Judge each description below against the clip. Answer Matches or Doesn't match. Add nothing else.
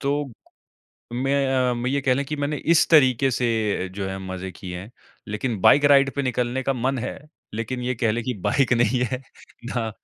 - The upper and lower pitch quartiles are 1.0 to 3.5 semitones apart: Matches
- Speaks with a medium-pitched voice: Doesn't match